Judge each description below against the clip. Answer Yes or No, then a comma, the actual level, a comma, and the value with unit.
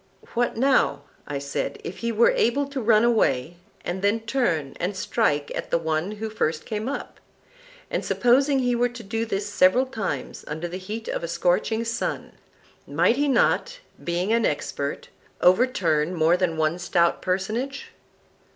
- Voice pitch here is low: No, high, 210 Hz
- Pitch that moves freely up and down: Yes, wide, 5.9 semitones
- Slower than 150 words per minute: No, average, 165 wpm